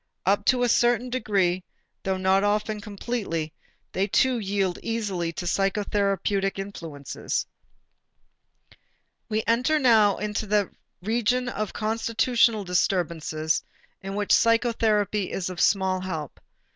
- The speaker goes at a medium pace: No, slow, 110 wpm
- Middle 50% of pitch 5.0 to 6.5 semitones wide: No, average, 3.3 semitones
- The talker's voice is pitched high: Yes, high, 205 Hz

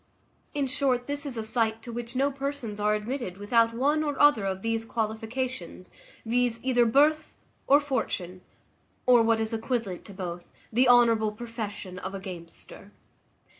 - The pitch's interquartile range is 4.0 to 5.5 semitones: No, average, 3.6 semitones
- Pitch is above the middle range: Yes, high, 230 Hz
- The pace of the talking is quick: No, average, 160 wpm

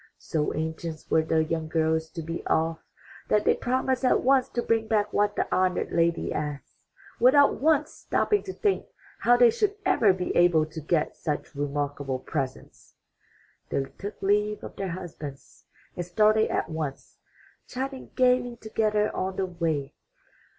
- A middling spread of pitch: No, wide, 6.9 semitones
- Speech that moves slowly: No, average, 155 wpm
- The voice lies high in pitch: No, medium, 180 Hz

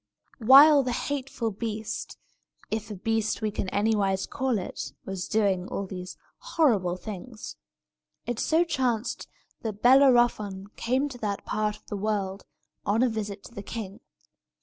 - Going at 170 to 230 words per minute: No, average, 150 wpm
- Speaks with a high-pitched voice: Yes, high, 220 Hz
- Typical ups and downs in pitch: Yes, average, 3.6 semitones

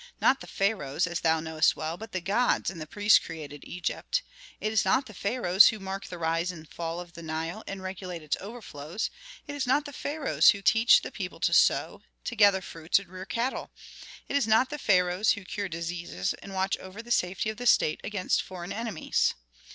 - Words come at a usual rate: No, fast, 210 wpm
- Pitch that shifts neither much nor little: Yes, average, 4.6 semitones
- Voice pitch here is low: No, high, 190 Hz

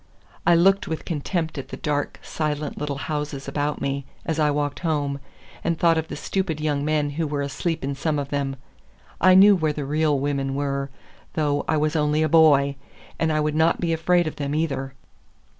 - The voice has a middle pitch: Yes, medium, 150 Hz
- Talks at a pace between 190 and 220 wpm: Yes, average, 200 wpm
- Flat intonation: Yes, narrow, 2.1 semitones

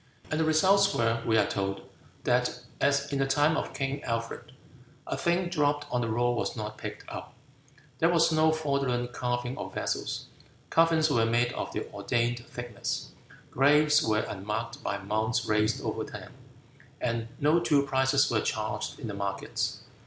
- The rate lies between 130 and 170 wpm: Yes, average, 165 wpm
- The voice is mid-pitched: No, low, 125 Hz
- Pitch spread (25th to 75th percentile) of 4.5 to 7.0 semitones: Yes, average, 4.8 semitones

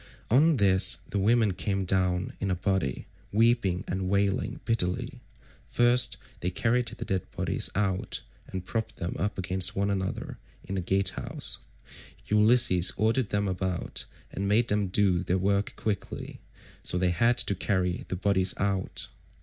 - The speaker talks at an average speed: Yes, average, 150 wpm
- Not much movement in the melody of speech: Yes, narrow, 2.3 semitones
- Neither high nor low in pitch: No, very low, 95 Hz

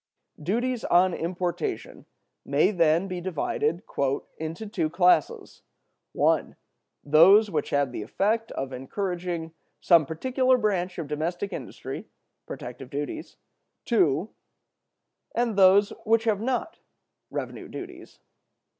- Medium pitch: Yes, medium, 180 Hz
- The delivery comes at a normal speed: No, slow, 110 wpm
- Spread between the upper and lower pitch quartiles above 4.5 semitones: Yes, average, 5.2 semitones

